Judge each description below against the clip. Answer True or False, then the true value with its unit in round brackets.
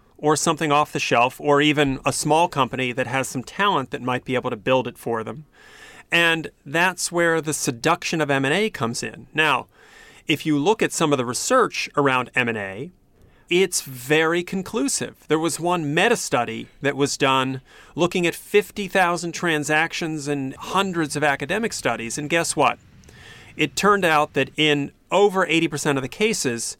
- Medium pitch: True (150 Hz)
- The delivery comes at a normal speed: True (170 wpm)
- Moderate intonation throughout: True (4.3 semitones)